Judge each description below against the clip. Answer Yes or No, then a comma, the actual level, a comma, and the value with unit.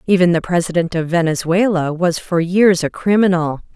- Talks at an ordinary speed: Yes, average, 160 wpm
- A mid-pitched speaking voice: Yes, medium, 175 Hz